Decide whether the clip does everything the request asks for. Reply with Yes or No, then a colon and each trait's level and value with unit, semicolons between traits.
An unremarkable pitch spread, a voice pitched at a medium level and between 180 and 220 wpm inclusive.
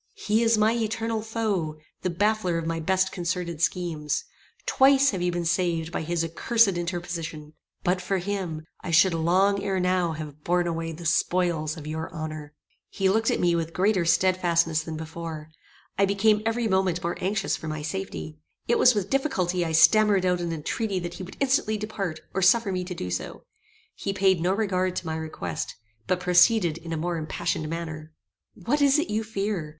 Yes: average, 3.5 semitones; medium, 180 Hz; average, 190 wpm